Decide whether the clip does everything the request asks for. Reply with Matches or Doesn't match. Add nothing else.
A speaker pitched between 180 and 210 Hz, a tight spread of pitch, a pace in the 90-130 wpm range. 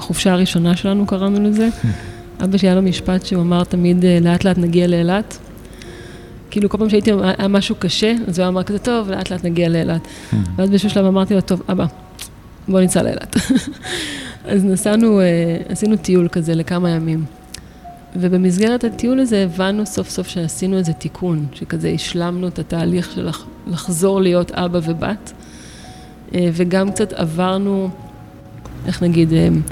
Doesn't match